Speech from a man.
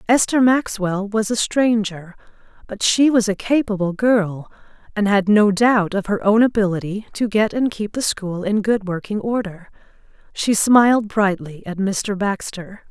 No: female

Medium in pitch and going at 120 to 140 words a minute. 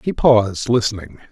No: low, 110 Hz; slow, 135 wpm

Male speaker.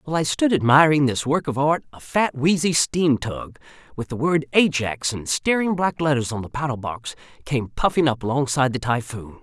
Yes: male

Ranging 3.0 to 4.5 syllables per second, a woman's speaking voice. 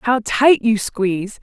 Yes: 3.9 syllables/s; female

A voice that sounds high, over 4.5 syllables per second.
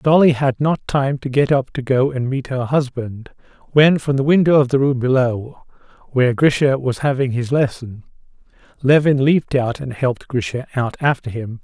No: low, 130 Hz; 5.0 syllables/s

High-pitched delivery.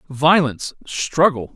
No: medium, 145 Hz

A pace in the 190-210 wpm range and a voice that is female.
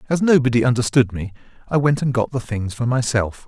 No: fast, 205 wpm; male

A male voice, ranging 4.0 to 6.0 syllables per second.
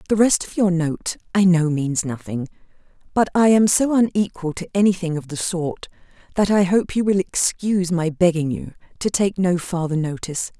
No: female; 5.1 syllables/s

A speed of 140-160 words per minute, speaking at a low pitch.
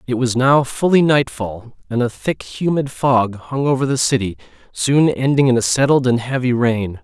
No: average, 195 wpm; low, 130 Hz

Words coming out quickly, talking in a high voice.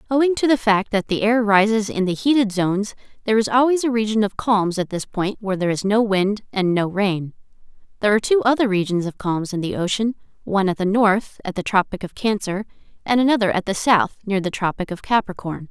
Yes: fast, 225 wpm; high, 205 Hz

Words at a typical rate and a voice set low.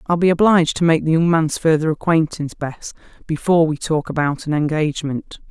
No: average, 185 wpm; medium, 160 Hz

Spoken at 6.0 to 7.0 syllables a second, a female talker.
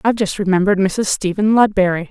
Yes: 6.5 syllables/s; female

